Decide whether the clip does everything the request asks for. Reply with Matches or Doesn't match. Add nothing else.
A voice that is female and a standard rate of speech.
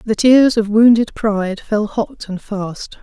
Matches